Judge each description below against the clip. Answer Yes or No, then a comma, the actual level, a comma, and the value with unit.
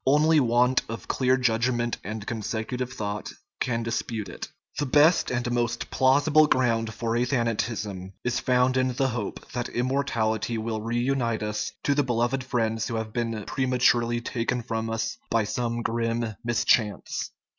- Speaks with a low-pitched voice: Yes, low, 120 Hz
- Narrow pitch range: Yes, narrow, 2.1 semitones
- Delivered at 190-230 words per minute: No, average, 155 wpm